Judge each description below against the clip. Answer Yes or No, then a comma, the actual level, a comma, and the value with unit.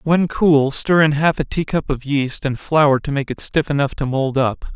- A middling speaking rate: No, fast, 250 wpm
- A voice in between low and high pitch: Yes, medium, 145 Hz